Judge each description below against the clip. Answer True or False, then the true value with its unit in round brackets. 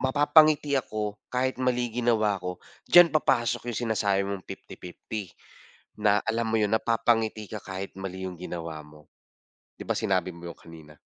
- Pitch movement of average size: True (4.4 semitones)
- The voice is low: True (110 Hz)